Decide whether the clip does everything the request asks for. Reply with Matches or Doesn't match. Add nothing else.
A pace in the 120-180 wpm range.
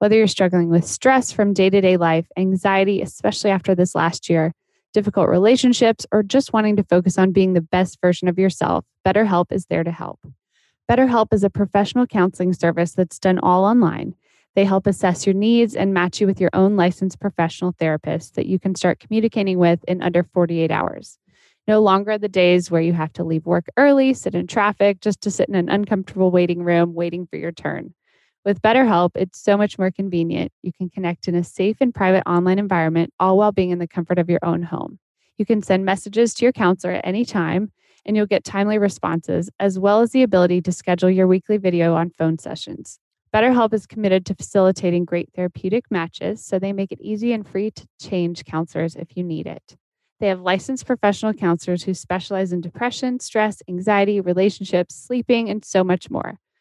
Doesn't match